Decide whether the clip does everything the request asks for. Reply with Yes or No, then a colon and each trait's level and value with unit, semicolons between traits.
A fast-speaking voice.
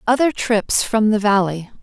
No: average, 165 wpm